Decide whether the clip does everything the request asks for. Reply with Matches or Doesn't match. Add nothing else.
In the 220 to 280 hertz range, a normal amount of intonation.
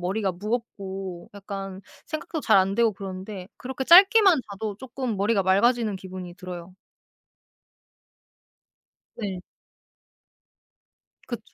Doesn't match